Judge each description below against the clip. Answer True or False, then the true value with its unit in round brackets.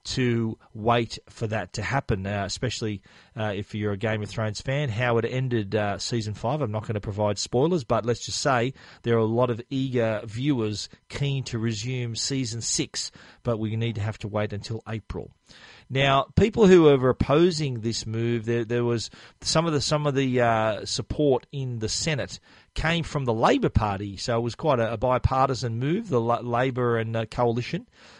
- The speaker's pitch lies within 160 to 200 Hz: False (120 Hz)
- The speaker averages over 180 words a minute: True (200 wpm)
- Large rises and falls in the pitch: False (3.2 semitones)